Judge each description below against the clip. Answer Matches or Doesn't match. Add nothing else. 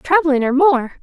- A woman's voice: Matches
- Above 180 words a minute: Doesn't match